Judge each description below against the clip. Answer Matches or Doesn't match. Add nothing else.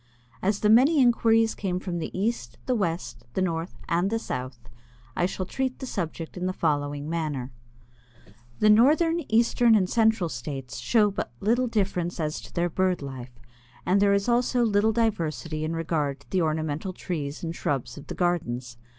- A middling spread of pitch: Doesn't match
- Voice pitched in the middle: Matches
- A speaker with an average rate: Matches